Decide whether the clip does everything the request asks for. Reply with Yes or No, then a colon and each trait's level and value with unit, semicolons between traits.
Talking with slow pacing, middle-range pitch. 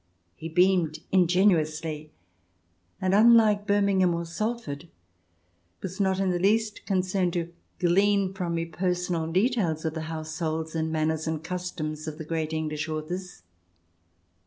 Yes: slow, 130 wpm; medium, 175 Hz